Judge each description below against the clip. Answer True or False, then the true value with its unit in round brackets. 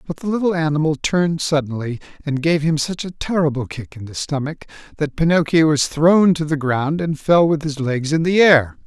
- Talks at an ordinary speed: False (210 wpm)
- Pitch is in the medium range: True (155 Hz)